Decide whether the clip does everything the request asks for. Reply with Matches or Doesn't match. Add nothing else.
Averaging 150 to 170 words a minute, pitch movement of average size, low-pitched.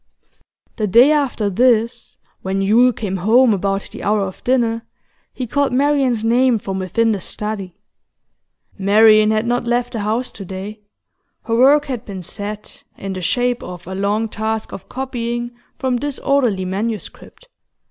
Doesn't match